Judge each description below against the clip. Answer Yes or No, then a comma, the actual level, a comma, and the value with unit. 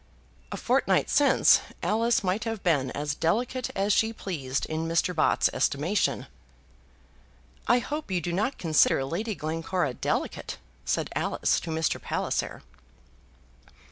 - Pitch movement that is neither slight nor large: No, wide, 5.9 semitones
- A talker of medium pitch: Yes, medium, 180 Hz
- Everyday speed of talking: No, slow, 130 wpm